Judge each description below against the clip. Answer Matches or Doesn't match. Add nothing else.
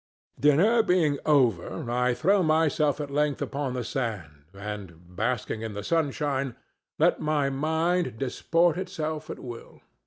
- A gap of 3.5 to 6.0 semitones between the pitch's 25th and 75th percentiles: Matches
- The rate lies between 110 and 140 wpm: Matches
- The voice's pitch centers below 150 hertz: Matches